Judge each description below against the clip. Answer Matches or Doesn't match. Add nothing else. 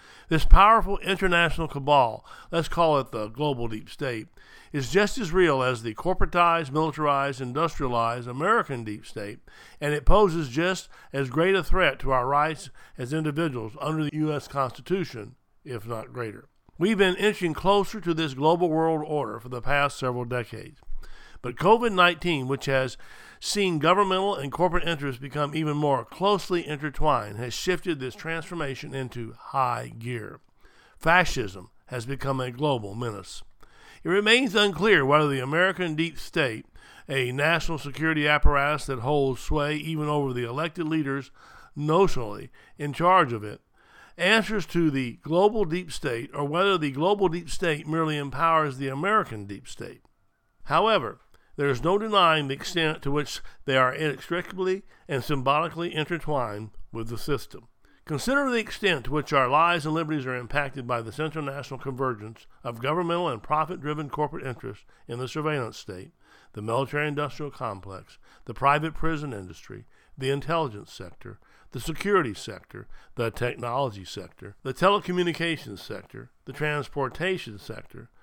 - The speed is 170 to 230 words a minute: Doesn't match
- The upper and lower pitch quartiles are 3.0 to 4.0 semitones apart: Doesn't match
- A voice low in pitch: Doesn't match